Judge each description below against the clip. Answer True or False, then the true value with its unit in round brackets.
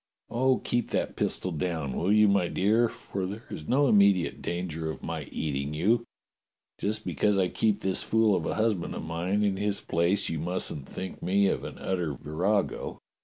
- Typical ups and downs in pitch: True (3.8 semitones)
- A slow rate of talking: False (180 wpm)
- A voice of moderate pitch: False (95 Hz)